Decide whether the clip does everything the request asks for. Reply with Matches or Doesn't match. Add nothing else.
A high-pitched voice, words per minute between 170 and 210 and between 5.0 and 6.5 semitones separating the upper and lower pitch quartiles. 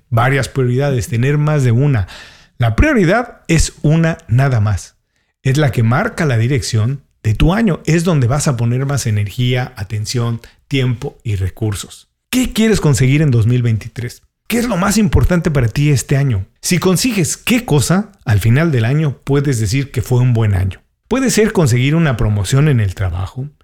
Doesn't match